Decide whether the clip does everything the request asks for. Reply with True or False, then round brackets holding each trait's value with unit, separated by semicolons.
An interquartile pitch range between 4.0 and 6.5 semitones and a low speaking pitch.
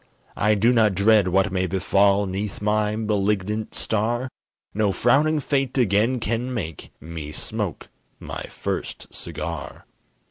False (3.2 semitones; 105 Hz)